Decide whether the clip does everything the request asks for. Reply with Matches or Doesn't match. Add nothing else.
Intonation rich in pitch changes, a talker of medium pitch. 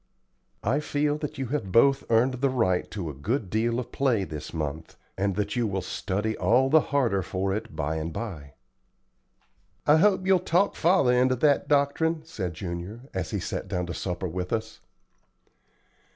Doesn't match